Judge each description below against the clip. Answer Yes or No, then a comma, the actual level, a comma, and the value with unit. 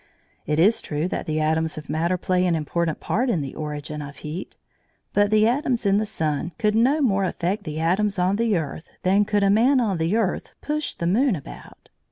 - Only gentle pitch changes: No, average, 5.2 semitones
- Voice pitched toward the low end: No, medium, 185 Hz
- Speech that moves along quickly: Yes, fast, 215 wpm